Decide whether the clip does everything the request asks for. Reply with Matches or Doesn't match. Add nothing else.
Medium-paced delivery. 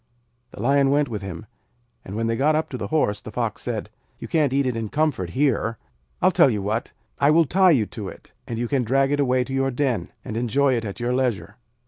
Doesn't match